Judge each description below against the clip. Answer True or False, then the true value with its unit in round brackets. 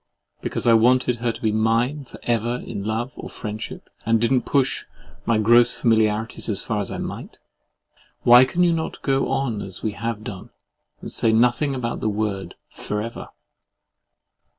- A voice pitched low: True (115 Hz)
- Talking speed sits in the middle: True (175 wpm)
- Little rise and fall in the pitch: True (2.3 semitones)